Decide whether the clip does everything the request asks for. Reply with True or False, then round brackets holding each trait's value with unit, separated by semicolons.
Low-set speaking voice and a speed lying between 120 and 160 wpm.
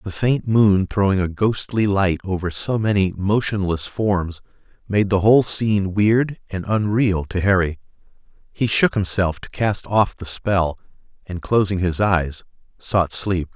True (100 Hz; 155 wpm)